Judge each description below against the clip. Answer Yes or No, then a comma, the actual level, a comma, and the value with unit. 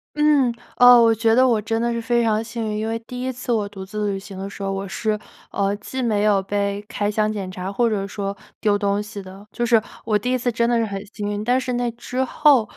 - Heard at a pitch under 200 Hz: No, high, 220 Hz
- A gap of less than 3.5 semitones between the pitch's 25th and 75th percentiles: Yes, average, 2.8 semitones